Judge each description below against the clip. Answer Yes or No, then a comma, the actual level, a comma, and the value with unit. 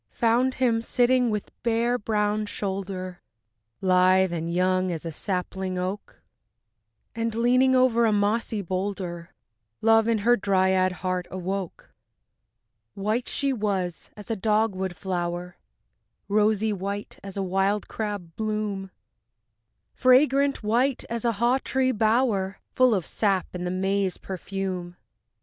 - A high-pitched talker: Yes, high, 205 Hz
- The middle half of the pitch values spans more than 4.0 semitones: No, average, 3.5 semitones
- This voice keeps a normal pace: No, slow, 130 wpm